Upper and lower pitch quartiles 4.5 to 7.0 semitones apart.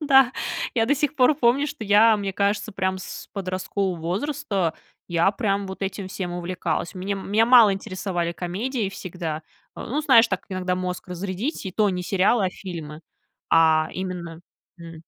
No: average, 3.5 semitones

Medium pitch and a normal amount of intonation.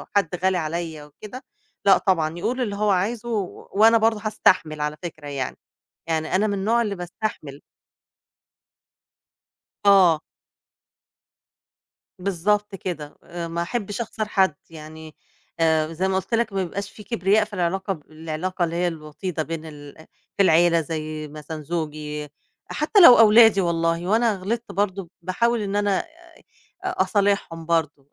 Yes: medium, 180 Hz; average, 4.4 semitones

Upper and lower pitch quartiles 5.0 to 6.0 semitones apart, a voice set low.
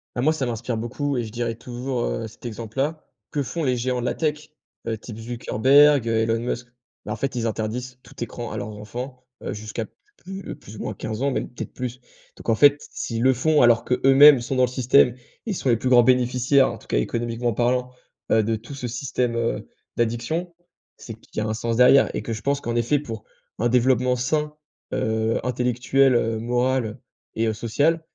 No: narrow, 2.5 semitones; low, 120 Hz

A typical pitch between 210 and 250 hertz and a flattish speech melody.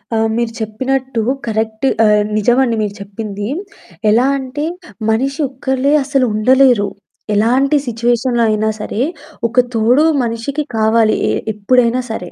No: high, 235 Hz; average, 3.2 semitones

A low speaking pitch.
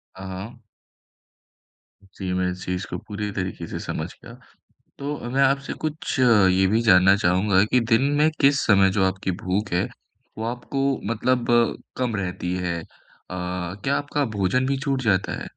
Yes: low, 100 Hz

